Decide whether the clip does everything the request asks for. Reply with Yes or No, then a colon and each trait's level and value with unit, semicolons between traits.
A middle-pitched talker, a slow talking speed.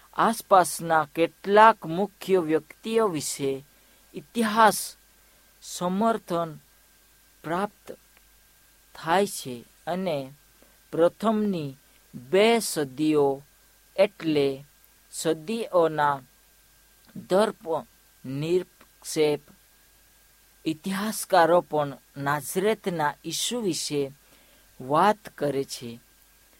Yes: medium, 165 Hz; slow, 55 wpm